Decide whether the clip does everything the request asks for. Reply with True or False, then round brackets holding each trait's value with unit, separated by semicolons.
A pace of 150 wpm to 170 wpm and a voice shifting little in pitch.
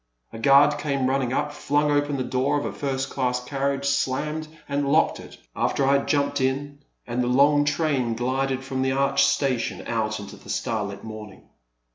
False (185 wpm; 2.3 semitones)